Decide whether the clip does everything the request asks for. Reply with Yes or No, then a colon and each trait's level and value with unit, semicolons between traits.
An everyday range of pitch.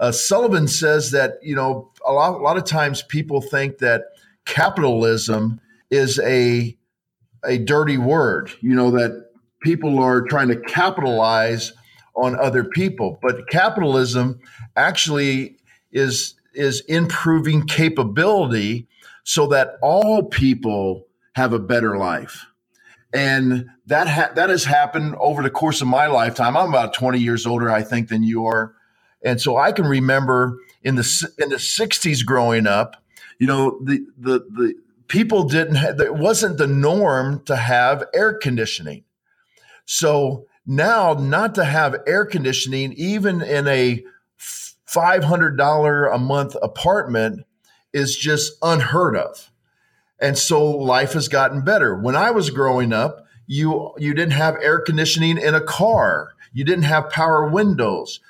Yes: average, 4.1 semitones